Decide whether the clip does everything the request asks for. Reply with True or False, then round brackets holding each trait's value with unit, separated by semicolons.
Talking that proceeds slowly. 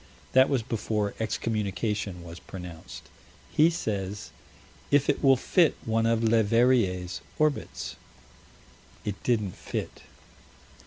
True (105 wpm)